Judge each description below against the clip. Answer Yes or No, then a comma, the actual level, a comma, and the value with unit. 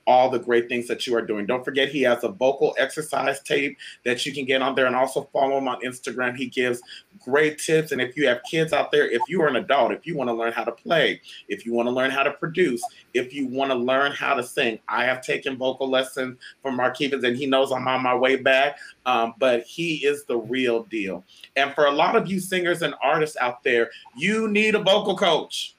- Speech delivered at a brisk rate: Yes, fast, 250 wpm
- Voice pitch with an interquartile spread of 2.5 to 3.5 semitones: No, average, 4.1 semitones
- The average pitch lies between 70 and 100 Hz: No, low, 135 Hz